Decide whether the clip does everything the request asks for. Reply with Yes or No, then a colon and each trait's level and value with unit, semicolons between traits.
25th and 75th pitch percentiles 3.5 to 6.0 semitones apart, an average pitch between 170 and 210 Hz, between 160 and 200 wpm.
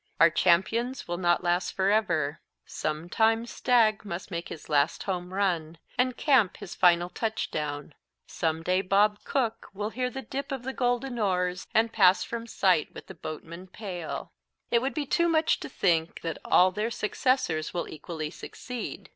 Yes: wide, 5.4 semitones; high, 190 Hz; average, 170 wpm